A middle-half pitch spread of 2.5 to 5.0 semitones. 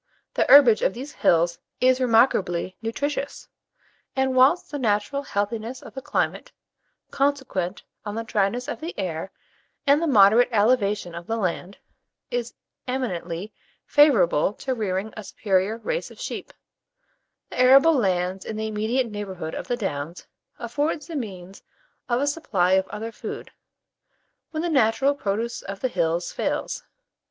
No: wide, 5.6 semitones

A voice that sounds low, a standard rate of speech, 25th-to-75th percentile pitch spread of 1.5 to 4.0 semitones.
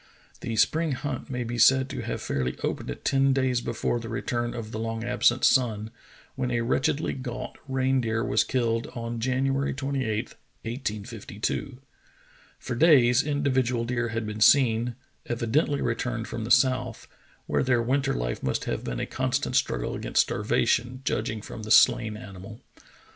Yes: low, 120 Hz; average, 160 wpm; average, 2.7 semitones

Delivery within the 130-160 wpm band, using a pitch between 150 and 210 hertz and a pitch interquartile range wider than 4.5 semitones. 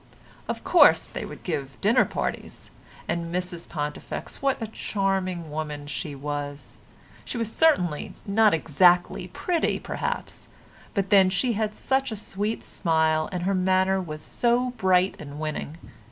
Yes: average, 145 wpm; medium, 185 Hz; average, 5.0 semitones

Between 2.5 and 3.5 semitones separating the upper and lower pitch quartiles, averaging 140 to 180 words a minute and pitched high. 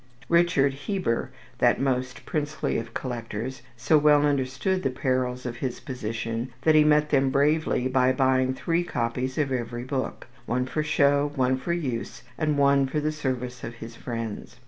No: average, 3.1 semitones; average, 170 wpm; low, 130 Hz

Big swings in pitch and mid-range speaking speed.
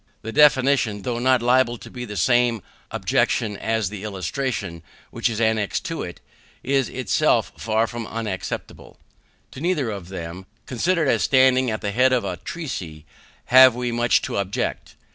No: average, 4.1 semitones; average, 160 wpm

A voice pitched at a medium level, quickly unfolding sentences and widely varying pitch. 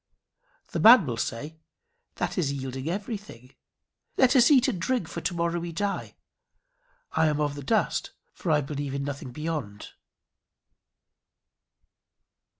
No: medium, 155 Hz; average, 140 wpm; wide, 5.9 semitones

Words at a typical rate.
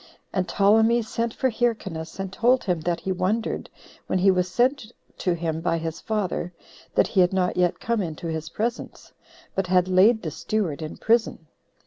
Yes: average, 180 wpm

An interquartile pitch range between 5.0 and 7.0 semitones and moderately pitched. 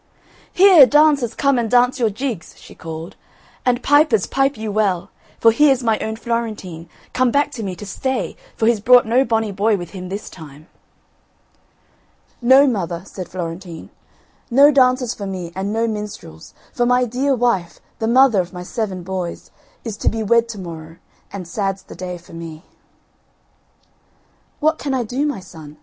No: wide, 5.5 semitones; high, 220 Hz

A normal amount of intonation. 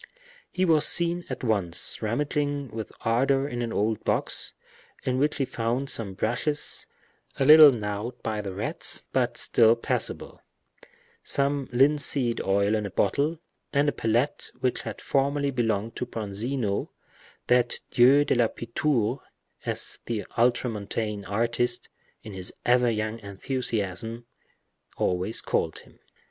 Yes: average, 4.3 semitones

